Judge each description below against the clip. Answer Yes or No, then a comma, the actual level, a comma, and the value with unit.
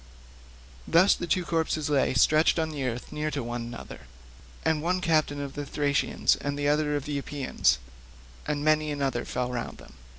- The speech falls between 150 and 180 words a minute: Yes, average, 175 wpm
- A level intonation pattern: Yes, narrow, 2.1 semitones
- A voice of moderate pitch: Yes, medium, 145 Hz